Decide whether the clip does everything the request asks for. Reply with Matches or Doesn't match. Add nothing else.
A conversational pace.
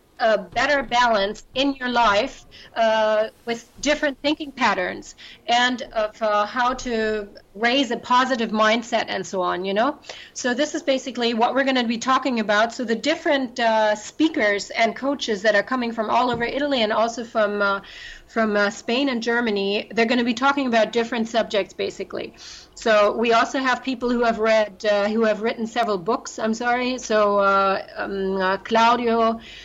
Matches